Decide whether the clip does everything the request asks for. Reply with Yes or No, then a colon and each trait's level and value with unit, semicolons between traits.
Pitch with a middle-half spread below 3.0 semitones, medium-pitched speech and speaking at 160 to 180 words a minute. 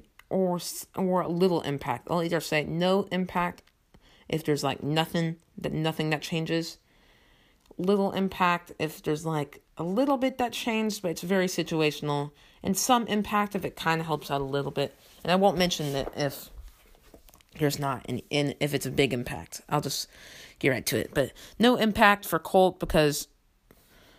No: average, 4.4 semitones; medium, 165 Hz; average, 175 wpm